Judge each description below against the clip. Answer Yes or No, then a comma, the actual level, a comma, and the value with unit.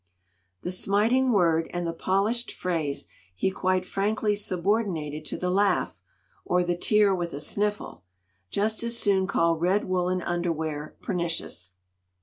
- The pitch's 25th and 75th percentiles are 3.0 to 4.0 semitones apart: Yes, average, 3.4 semitones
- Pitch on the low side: No, medium, 185 Hz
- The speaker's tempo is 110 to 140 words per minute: Yes, slow, 135 wpm